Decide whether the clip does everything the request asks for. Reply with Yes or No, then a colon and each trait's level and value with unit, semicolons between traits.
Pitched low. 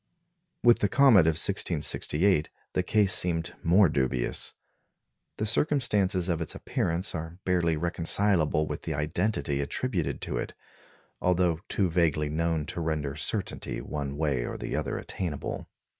Yes: very low, 85 Hz